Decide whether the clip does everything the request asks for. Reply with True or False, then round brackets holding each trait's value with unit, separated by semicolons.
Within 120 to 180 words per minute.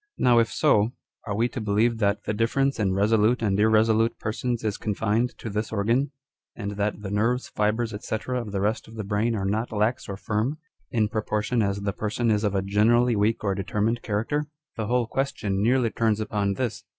False (200 wpm)